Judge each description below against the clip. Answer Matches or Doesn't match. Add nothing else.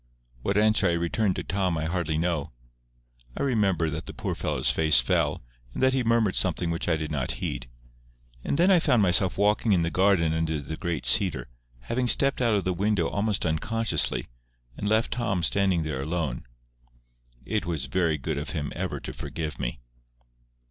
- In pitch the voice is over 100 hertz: Doesn't match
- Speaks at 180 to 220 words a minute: Matches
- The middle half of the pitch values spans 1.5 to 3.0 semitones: Doesn't match